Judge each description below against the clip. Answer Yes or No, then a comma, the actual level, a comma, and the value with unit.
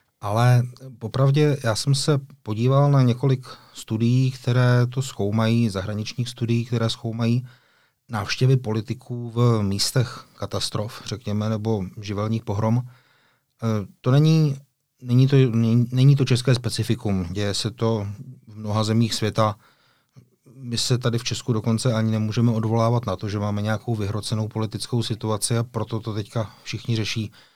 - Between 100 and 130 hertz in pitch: Yes, low, 115 Hz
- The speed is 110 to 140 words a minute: Yes, average, 135 wpm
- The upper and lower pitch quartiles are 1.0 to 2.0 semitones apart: No, narrow, 2.6 semitones